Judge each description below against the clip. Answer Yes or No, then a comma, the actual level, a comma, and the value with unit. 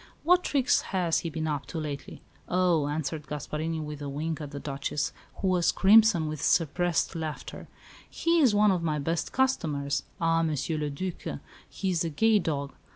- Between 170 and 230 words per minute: Yes, average, 180 wpm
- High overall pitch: No, medium, 160 Hz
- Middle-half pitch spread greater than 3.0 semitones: Yes, average, 3.7 semitones